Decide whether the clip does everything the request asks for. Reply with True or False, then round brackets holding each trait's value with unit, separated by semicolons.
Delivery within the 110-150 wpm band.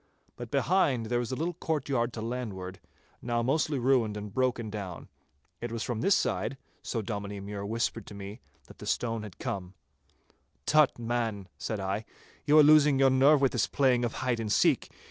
False (185 wpm)